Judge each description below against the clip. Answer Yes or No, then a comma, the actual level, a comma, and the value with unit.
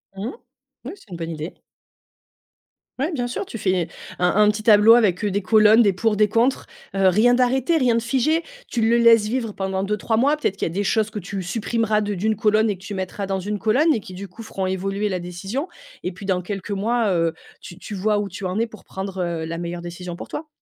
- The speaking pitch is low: No, high, 210 Hz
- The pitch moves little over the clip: No, average, 3.3 semitones